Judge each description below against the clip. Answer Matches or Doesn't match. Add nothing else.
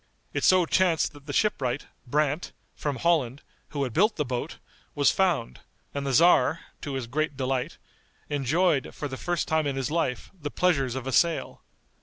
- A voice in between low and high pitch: Matches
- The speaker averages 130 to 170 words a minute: Doesn't match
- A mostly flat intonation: Doesn't match